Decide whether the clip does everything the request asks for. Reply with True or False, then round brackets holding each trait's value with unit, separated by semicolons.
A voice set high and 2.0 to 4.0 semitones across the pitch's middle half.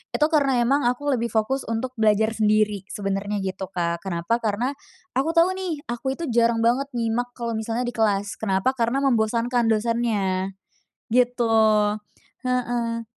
True (230 Hz; 2.9 semitones)